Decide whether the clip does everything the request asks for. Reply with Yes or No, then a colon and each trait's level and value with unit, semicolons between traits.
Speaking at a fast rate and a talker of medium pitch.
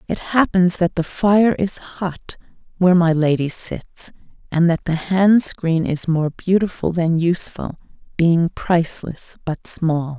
No: average, 145 wpm; medium, 170 Hz